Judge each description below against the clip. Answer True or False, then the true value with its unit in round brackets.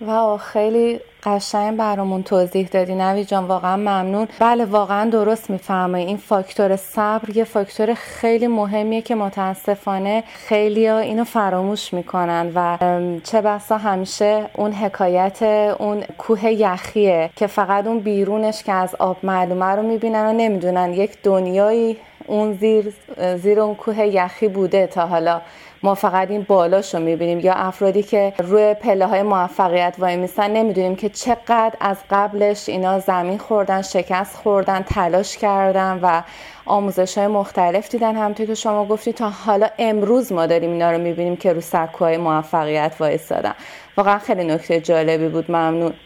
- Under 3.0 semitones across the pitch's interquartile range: True (2.6 semitones)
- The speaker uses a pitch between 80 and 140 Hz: False (200 Hz)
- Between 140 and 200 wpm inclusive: True (150 wpm)